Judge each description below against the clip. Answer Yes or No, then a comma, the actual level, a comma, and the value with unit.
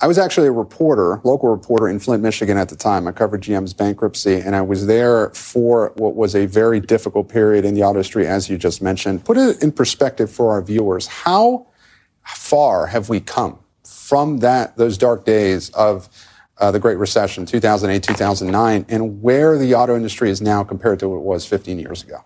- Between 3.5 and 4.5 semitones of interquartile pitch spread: No, average, 3.1 semitones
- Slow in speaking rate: No, average, 200 wpm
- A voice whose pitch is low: Yes, low, 105 Hz